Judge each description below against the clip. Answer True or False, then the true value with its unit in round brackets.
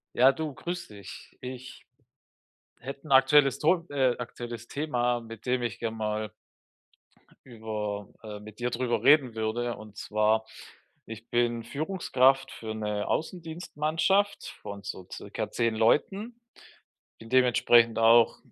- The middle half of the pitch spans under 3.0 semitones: False (3.9 semitones)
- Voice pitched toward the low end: True (120 Hz)